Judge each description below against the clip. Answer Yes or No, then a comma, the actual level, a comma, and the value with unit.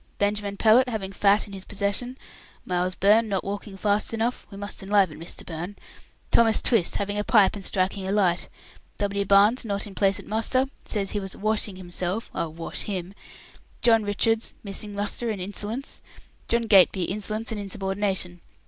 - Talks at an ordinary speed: Yes, average, 170 wpm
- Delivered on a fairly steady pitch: Yes, narrow, 2.1 semitones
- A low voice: No, high, 205 Hz